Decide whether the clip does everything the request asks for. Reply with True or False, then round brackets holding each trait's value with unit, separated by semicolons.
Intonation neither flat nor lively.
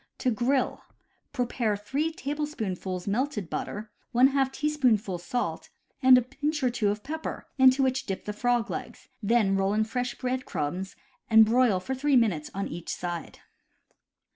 True (4.7 semitones)